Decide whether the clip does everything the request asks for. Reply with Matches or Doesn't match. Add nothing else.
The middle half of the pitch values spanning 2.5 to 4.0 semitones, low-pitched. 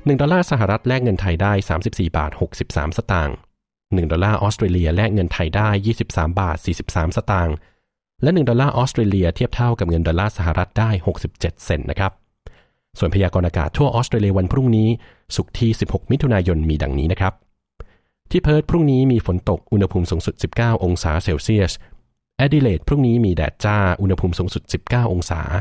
Doesn't match